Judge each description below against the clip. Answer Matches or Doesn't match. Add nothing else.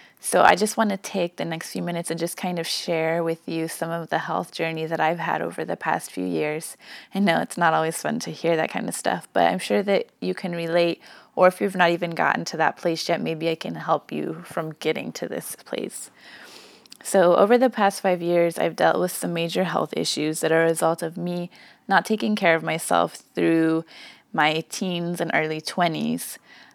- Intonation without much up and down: Matches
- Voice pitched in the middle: Matches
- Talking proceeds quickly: Matches